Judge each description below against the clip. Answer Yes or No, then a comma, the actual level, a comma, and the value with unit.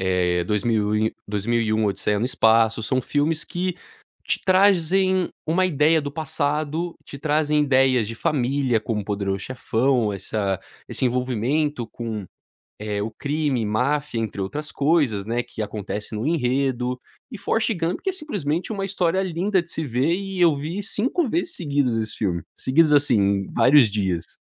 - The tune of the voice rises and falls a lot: Yes, wide, 6.8 semitones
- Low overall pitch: Yes, low, 130 Hz